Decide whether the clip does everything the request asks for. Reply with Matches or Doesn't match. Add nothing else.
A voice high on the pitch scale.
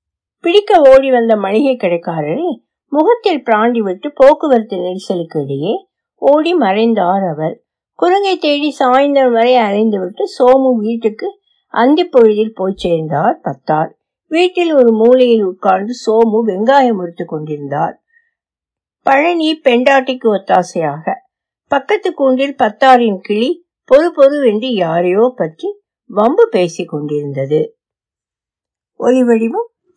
Matches